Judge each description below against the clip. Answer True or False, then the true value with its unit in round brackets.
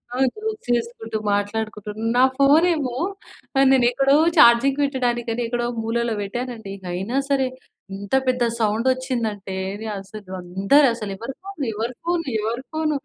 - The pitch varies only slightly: False (4.0 semitones)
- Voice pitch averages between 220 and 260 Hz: True (240 Hz)